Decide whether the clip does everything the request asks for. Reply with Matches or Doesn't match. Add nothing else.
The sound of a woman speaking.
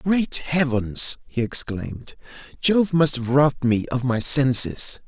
Doesn't match